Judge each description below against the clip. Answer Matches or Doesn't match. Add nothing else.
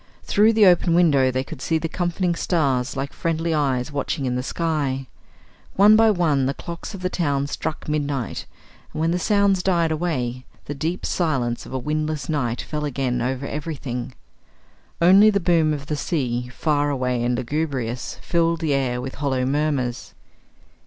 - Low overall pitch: Doesn't match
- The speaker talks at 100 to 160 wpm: Doesn't match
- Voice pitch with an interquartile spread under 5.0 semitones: Matches